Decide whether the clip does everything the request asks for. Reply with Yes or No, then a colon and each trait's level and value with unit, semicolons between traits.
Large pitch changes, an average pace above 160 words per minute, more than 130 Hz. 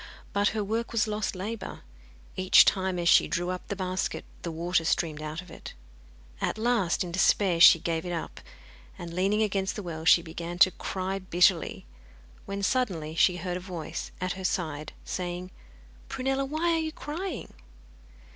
No: average, 3.4 semitones; average, 175 wpm; medium, 185 Hz